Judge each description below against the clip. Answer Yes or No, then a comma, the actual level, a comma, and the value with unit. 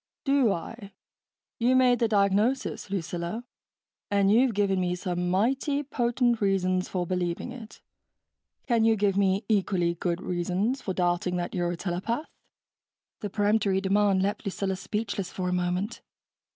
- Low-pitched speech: No, high, 200 Hz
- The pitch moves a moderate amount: Yes, average, 3.8 semitones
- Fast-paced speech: No, average, 145 wpm